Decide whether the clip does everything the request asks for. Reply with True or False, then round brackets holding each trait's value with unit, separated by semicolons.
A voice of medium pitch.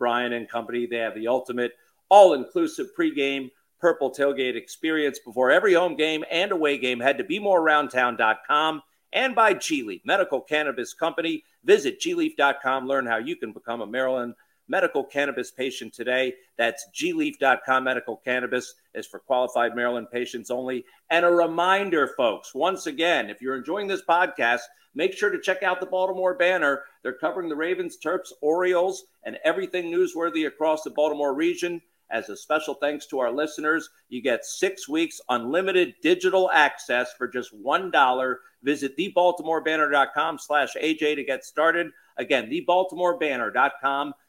True (155 Hz)